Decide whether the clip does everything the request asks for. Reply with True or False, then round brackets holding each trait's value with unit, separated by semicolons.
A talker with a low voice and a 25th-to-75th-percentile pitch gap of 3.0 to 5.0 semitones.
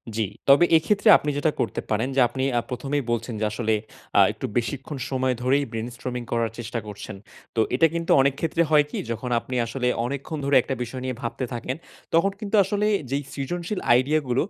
True (130 Hz; 3.9 semitones)